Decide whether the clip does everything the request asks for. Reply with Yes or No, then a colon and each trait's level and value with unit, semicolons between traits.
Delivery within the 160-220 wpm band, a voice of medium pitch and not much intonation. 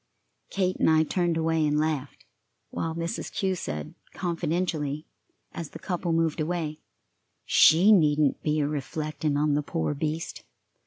No: average, 145 wpm; medium, 160 Hz; narrow, 2.2 semitones